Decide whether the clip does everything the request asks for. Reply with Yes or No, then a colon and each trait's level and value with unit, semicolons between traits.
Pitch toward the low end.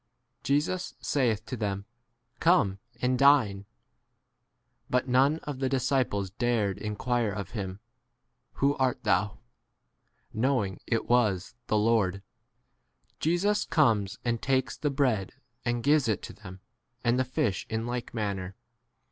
Yes: low, 120 Hz